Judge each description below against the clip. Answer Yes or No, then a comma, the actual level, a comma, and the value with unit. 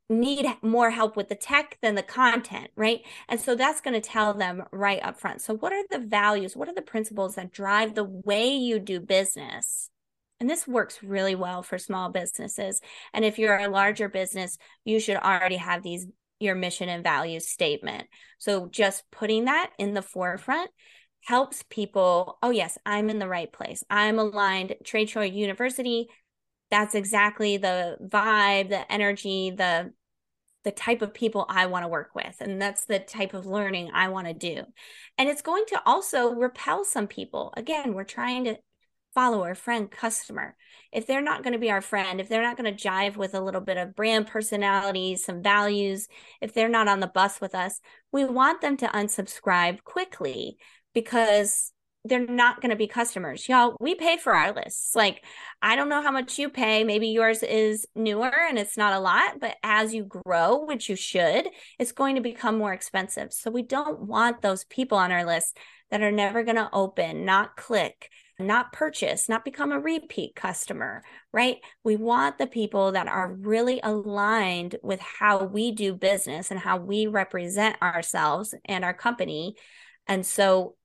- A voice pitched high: Yes, high, 210 Hz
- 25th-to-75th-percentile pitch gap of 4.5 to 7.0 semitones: No, average, 3.6 semitones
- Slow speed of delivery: No, average, 185 wpm